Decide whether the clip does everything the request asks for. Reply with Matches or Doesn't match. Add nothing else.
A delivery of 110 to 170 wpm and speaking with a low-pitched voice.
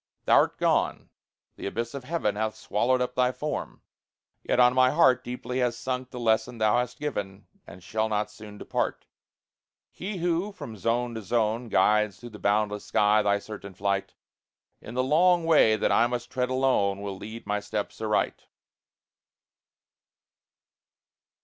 Matches